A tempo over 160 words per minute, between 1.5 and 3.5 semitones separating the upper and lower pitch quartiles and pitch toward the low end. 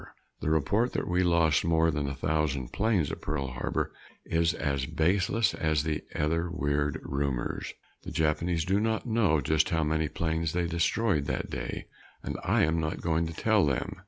Yes: average, 180 wpm; average, 2.8 semitones; very low, 80 Hz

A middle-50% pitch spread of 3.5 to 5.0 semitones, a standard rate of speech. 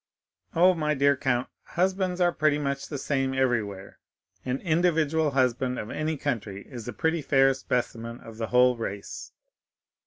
Yes: average, 4.3 semitones; average, 155 wpm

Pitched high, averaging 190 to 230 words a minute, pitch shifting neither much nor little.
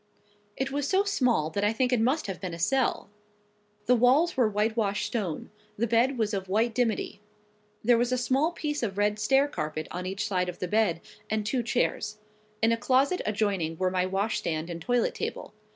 Yes: high, 220 Hz; average, 195 wpm; average, 4.7 semitones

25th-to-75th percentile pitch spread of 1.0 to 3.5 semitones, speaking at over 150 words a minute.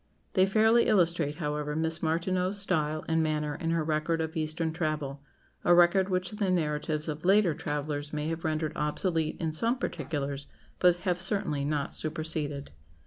Yes: average, 3.0 semitones; average, 160 wpm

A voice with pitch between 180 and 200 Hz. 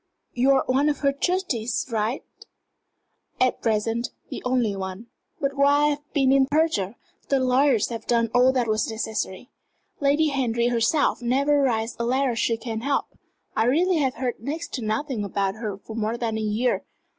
No: high, 245 Hz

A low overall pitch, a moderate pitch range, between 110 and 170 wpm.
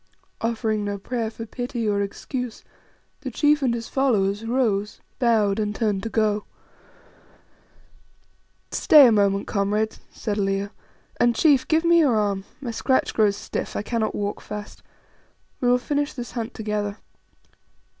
No: high, 220 Hz; average, 3.3 semitones; average, 145 wpm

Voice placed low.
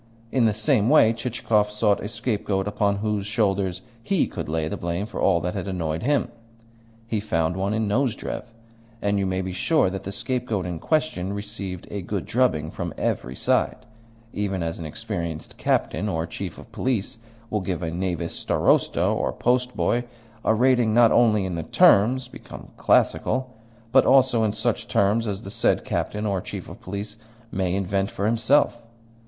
Yes: low, 105 Hz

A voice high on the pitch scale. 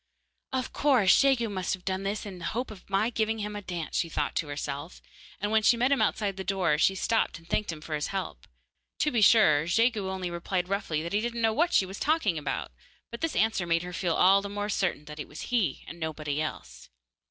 Yes: high, 195 Hz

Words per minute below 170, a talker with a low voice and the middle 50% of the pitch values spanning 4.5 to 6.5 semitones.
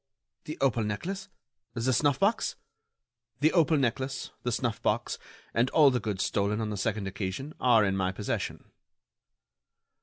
Yes: average, 150 wpm; low, 120 Hz; average, 5.0 semitones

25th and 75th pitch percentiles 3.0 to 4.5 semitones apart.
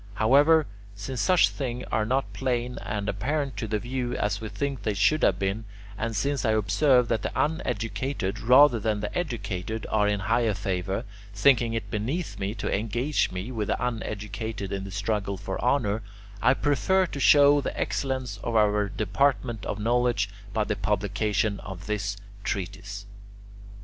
Yes: average, 4.1 semitones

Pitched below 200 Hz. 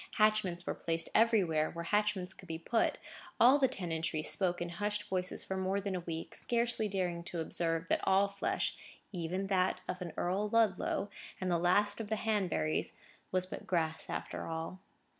Yes: medium, 185 Hz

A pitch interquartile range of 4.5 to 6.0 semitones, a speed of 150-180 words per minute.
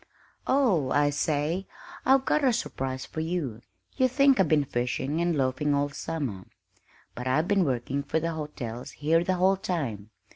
Yes: wide, 5.4 semitones; average, 170 wpm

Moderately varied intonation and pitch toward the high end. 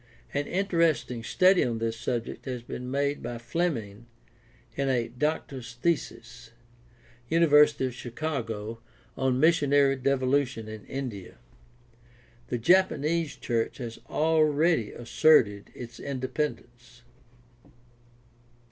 No: average, 4.2 semitones; low, 130 Hz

